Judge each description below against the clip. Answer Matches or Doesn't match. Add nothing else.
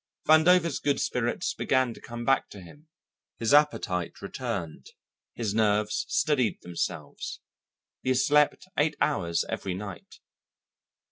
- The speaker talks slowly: Matches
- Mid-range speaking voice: Doesn't match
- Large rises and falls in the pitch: Matches